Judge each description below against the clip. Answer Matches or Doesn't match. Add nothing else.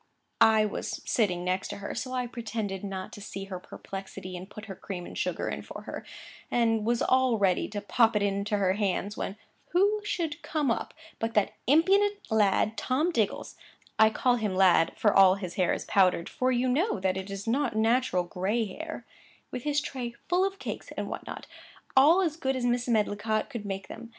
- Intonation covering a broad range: Doesn't match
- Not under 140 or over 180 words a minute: Doesn't match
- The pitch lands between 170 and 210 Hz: Doesn't match